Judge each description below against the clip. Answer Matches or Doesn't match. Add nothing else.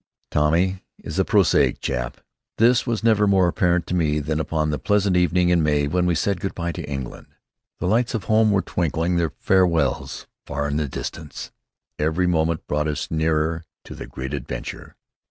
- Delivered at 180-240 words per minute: Matches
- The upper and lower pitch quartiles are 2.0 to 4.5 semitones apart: Matches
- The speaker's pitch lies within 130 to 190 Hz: Doesn't match